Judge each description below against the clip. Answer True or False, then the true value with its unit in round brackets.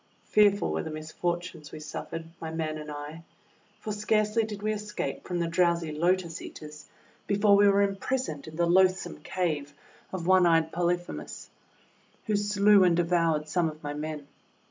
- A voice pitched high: False (175 Hz)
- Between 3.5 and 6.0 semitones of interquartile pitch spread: True (4.3 semitones)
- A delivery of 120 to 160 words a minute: False (170 wpm)